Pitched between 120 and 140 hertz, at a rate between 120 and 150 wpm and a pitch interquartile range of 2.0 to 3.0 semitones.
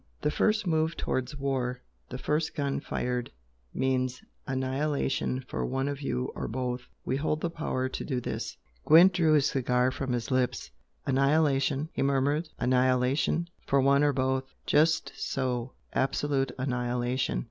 Yes: low, 135 Hz; average, 145 wpm; narrow, 2.5 semitones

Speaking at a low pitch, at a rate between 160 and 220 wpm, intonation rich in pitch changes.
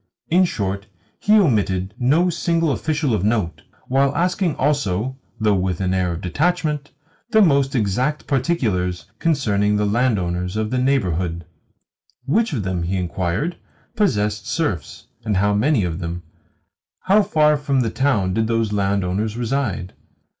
No: low, 110 Hz; average, 145 wpm; wide, 7.5 semitones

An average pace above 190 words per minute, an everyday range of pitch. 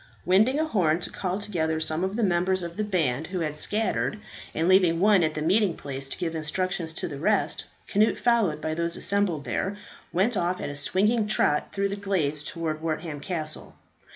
Yes: average, 200 wpm; average, 4.2 semitones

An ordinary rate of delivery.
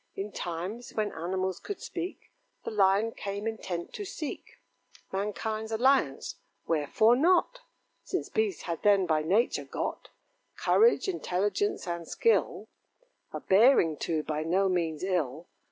No: slow, 130 wpm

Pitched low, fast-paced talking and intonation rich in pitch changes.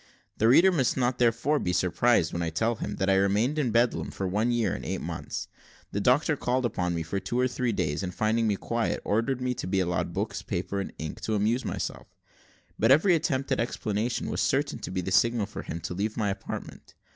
No: low, 110 Hz; fast, 225 wpm; average, 4.2 semitones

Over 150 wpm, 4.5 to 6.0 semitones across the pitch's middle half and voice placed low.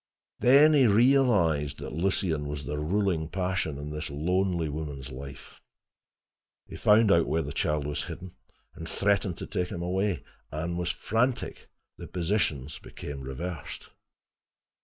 No: average, 140 wpm; average, 5.0 semitones; very low, 85 Hz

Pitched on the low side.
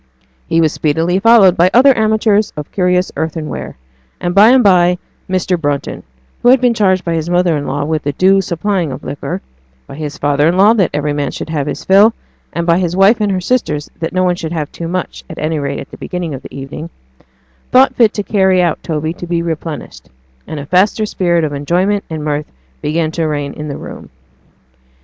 No: medium, 170 Hz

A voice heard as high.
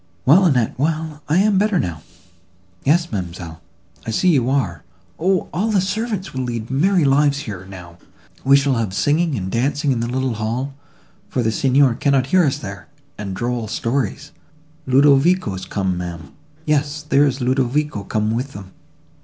No: low, 135 Hz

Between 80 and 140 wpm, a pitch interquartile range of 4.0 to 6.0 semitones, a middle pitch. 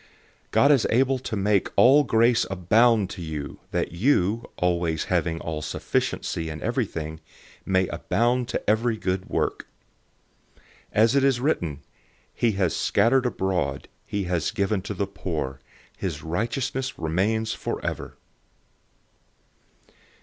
No: slow, 135 wpm; wide, 5.6 semitones; low, 100 Hz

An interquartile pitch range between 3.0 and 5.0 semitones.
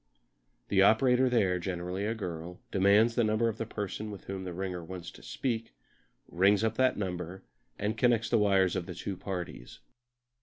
Yes: average, 3.5 semitones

